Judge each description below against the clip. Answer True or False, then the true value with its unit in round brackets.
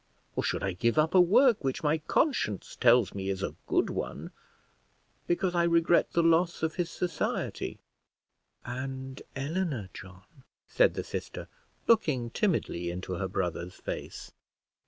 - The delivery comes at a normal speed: True (145 wpm)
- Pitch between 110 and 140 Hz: True (135 Hz)